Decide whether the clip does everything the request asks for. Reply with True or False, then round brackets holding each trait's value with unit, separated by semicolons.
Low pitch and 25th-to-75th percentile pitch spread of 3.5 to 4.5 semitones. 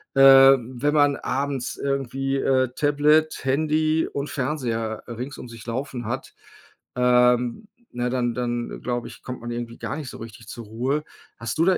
False (130 Hz; 2.9 semitones)